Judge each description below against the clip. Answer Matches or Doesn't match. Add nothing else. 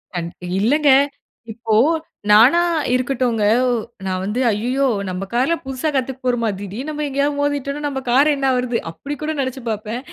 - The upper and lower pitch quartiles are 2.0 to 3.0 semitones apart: Doesn't match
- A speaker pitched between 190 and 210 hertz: Doesn't match